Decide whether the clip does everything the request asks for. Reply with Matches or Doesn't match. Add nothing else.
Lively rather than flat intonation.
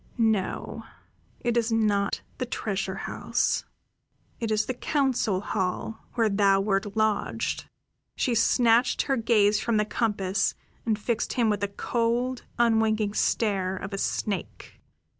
Doesn't match